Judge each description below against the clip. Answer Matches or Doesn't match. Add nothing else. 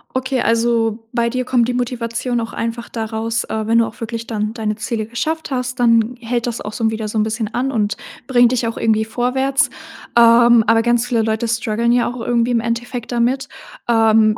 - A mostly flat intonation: Matches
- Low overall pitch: Doesn't match